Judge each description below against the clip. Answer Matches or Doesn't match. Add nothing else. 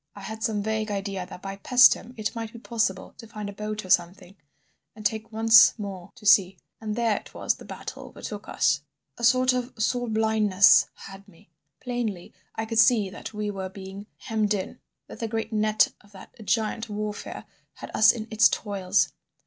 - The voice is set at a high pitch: Matches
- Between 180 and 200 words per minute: Matches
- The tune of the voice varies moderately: Doesn't match